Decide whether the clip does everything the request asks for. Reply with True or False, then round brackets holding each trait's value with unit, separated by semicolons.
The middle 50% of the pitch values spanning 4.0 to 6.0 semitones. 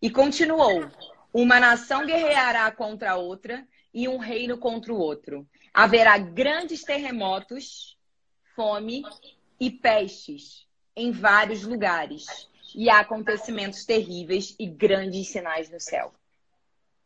True (4.3 semitones)